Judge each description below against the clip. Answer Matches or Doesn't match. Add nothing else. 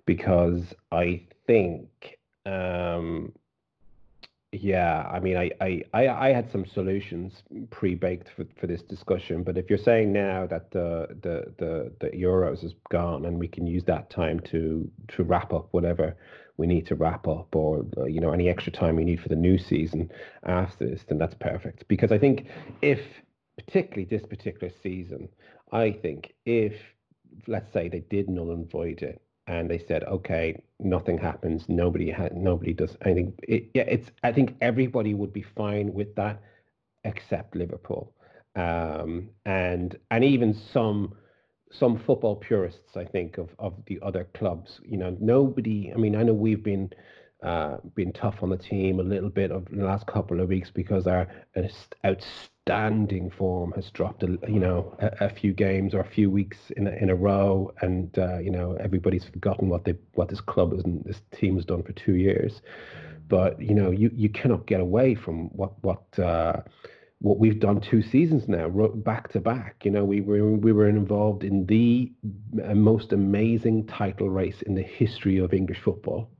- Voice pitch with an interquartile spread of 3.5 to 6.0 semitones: Doesn't match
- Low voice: Matches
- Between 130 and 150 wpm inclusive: Doesn't match